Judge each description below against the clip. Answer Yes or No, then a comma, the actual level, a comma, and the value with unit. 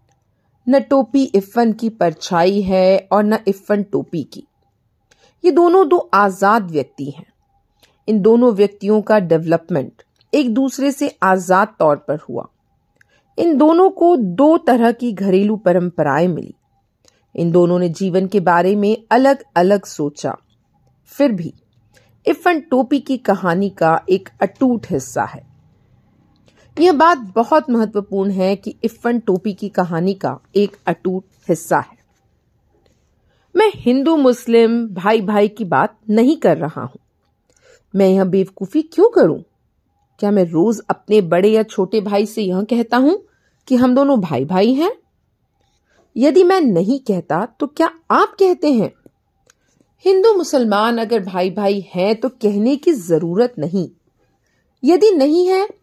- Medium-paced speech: Yes, average, 140 wpm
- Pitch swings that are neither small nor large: No, wide, 6.3 semitones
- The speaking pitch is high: Yes, high, 210 Hz